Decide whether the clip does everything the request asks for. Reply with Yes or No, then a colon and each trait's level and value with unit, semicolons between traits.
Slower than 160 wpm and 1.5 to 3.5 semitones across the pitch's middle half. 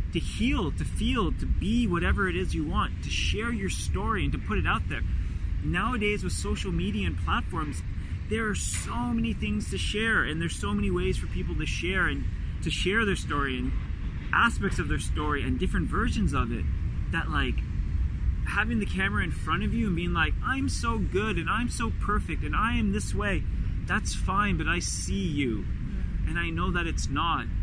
No: fast, 205 wpm; average, 3.2 semitones